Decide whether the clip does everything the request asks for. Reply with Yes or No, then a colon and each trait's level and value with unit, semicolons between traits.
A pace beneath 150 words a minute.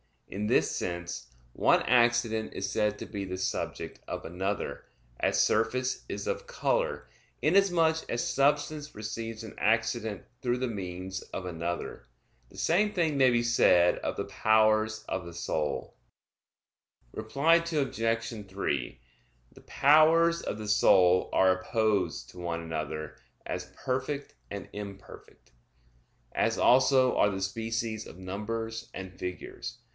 Yes: slow, 135 wpm